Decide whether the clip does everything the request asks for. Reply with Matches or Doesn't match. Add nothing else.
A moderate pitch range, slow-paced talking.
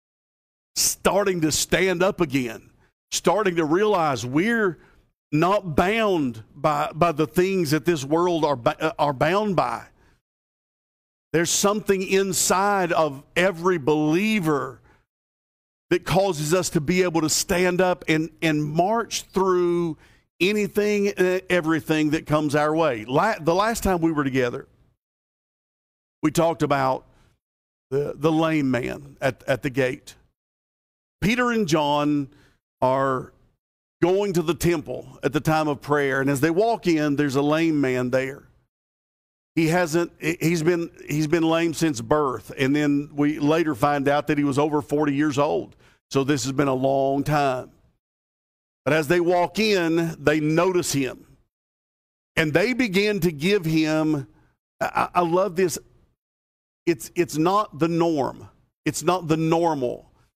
Doesn't match